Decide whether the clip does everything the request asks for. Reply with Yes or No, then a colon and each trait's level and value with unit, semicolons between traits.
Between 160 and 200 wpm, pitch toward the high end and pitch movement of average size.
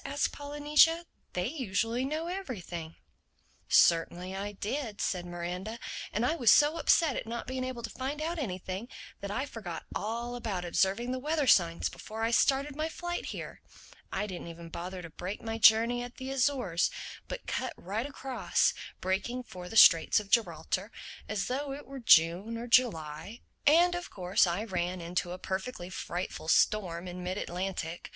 No: average, 170 wpm; high, 220 Hz; wide, 6.4 semitones